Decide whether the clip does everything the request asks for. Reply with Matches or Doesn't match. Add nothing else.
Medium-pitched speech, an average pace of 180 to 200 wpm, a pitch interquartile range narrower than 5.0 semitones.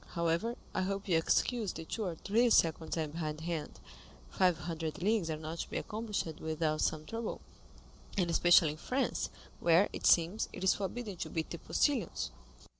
Matches